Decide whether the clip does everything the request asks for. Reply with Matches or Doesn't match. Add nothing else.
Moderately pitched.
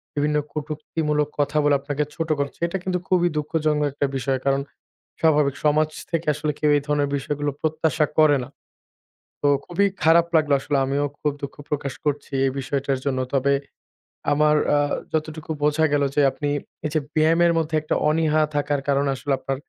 Matches